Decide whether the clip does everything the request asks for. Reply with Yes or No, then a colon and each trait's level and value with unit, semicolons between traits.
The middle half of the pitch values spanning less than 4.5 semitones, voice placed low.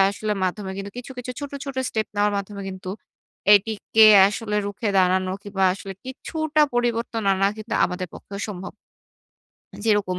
No: average, 2.9 semitones; high, 205 Hz